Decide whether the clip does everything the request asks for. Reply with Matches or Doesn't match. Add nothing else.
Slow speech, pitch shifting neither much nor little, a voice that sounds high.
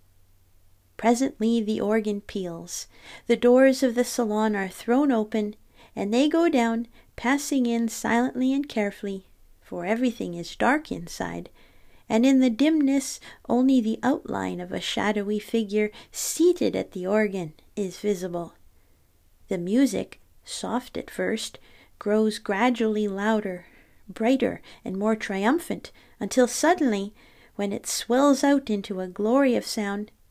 Matches